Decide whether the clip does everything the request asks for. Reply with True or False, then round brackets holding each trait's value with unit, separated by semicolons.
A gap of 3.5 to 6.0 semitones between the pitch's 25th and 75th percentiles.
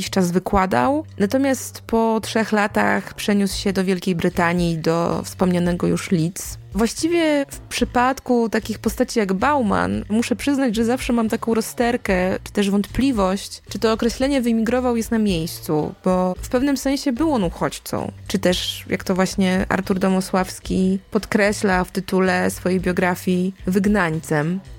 True (4.3 semitones)